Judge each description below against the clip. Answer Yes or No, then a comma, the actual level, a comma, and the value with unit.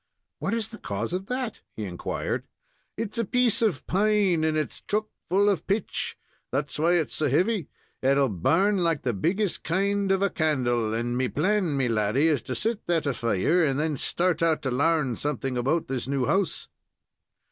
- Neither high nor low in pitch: Yes, medium, 160 Hz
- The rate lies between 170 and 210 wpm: Yes, average, 180 wpm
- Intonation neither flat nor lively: No, wide, 6.9 semitones